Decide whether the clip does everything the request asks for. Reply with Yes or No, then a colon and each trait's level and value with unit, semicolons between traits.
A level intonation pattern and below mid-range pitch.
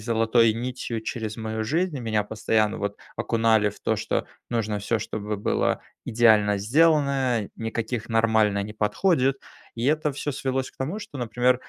No: average, 3.2 semitones; low, 115 Hz